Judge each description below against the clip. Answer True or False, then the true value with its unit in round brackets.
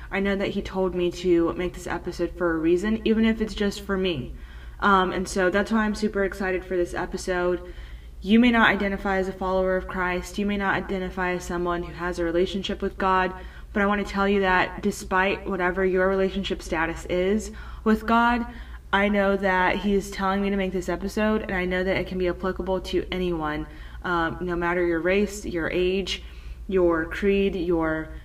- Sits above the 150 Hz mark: True (185 Hz)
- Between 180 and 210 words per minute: True (205 wpm)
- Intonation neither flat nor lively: False (1.9 semitones)